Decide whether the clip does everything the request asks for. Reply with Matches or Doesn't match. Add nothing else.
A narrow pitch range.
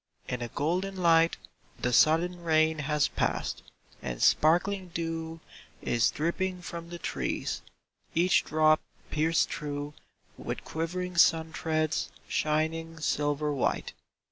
Matches